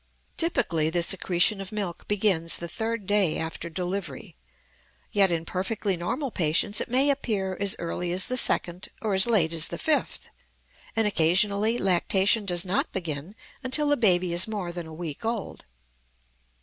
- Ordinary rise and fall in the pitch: Yes, average, 3.8 semitones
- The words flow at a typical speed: Yes, average, 160 wpm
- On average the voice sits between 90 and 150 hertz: No, high, 190 Hz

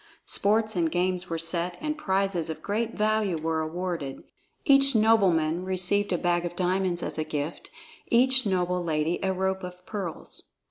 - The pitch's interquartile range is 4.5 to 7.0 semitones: No, average, 3.2 semitones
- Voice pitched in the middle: Yes, medium, 180 Hz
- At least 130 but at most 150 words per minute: No, average, 165 wpm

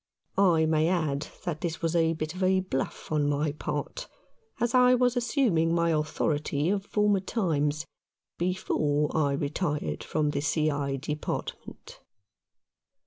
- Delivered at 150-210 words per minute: No, average, 140 wpm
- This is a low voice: No, medium, 155 Hz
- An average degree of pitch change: Yes, average, 3.8 semitones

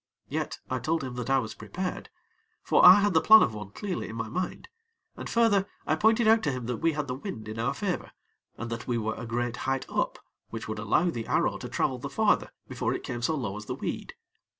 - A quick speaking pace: Yes, fast, 245 wpm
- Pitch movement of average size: No, wide, 7.9 semitones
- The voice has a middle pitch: No, low, 130 Hz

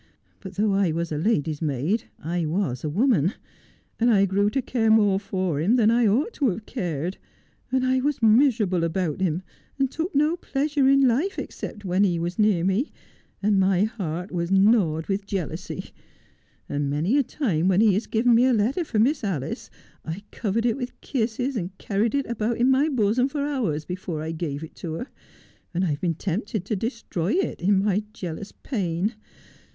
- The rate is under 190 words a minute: No, average, 195 wpm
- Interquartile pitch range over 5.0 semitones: Yes, wide, 5.6 semitones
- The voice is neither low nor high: No, high, 200 Hz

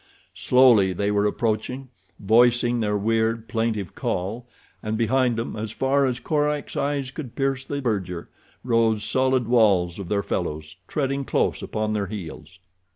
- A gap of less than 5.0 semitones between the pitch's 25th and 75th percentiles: Yes, average, 4.0 semitones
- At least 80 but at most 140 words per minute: No, average, 150 wpm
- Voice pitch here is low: Yes, low, 115 Hz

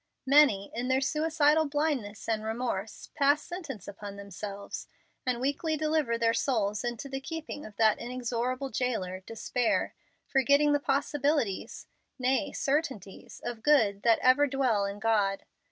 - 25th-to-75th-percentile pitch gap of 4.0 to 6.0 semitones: Yes, average, 5.1 semitones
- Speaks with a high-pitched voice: Yes, very high, 250 Hz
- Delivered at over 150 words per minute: No, slow, 135 wpm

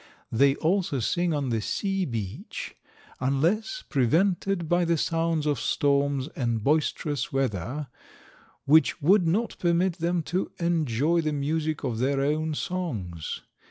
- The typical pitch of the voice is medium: Yes, medium, 155 Hz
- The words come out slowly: Yes, slow, 130 wpm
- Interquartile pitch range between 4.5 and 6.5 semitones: No, average, 4.1 semitones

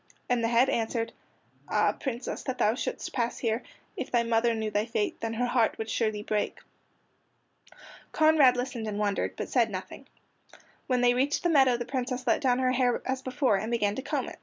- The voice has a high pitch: Yes, high, 240 Hz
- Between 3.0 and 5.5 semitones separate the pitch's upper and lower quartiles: No, narrow, 2.5 semitones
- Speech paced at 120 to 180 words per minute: No, average, 200 wpm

